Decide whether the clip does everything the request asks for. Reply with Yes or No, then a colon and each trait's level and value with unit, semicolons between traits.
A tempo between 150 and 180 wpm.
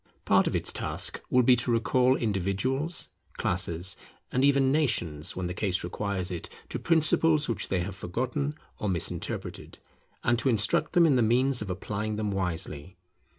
Yes: average, 165 wpm